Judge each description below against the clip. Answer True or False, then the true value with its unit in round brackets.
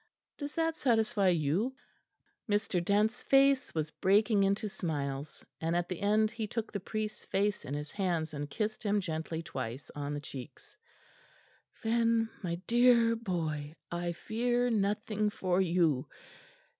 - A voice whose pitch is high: True (200 Hz)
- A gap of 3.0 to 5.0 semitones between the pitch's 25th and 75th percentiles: False (5.5 semitones)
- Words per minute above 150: False (145 wpm)